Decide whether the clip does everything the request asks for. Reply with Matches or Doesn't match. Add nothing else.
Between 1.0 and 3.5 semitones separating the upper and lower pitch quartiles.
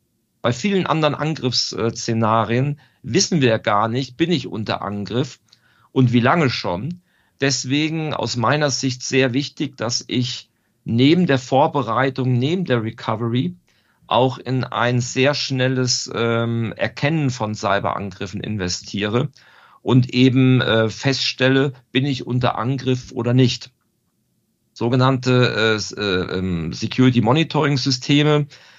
Matches